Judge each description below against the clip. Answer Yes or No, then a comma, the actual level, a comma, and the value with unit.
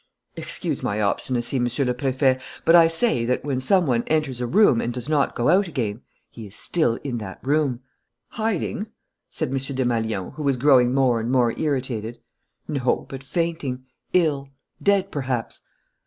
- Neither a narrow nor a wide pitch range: Yes, average, 4.0 semitones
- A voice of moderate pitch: No, low, 130 Hz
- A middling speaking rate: Yes, average, 170 wpm